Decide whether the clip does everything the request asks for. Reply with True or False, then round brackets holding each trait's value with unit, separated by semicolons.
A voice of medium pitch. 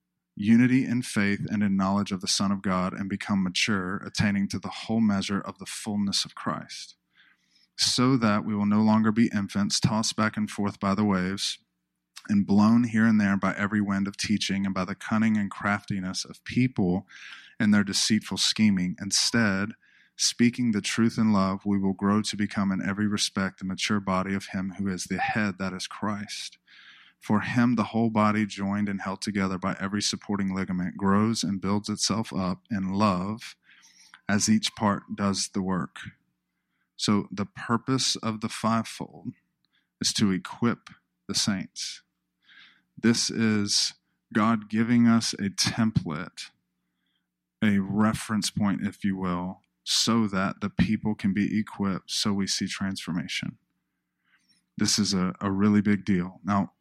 False (100 Hz)